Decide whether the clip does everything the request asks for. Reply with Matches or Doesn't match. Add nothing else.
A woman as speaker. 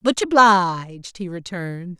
Matches